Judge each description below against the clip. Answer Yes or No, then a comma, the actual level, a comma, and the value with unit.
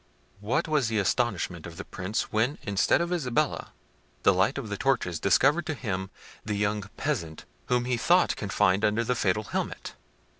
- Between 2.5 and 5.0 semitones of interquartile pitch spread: No, wide, 5.4 semitones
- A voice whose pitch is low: Yes, low, 110 Hz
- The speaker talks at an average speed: Yes, average, 175 wpm